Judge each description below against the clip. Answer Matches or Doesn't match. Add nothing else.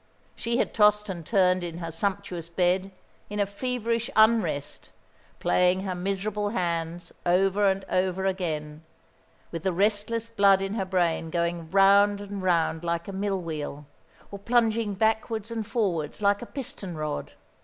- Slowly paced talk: Doesn't match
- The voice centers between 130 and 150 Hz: Doesn't match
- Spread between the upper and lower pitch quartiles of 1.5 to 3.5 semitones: Matches